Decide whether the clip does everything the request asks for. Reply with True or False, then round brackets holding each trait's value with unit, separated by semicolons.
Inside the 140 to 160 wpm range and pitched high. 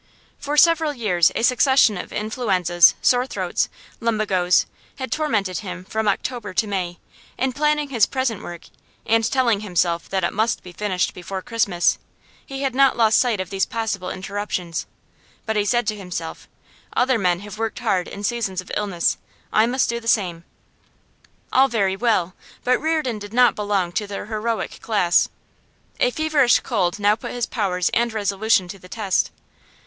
False (170 wpm; 215 Hz)